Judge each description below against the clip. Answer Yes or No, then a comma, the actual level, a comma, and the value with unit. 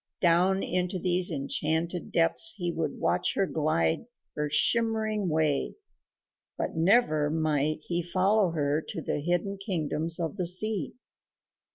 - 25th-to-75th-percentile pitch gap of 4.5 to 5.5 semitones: No, average, 3.6 semitones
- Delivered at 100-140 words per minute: Yes, slow, 135 wpm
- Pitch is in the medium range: Yes, medium, 170 Hz